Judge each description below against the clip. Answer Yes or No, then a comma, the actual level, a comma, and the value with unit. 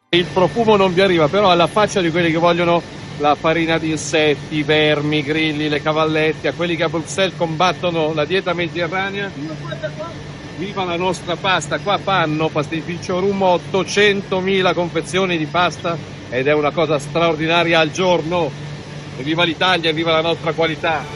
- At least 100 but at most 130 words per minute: No, average, 160 wpm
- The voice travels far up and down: No, average, 2.7 semitones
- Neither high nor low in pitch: Yes, medium, 165 Hz